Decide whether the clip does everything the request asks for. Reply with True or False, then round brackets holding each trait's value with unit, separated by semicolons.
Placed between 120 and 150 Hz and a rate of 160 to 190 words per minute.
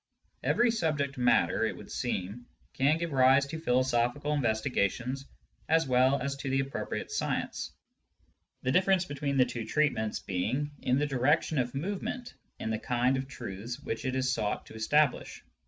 True (135 Hz; 165 wpm)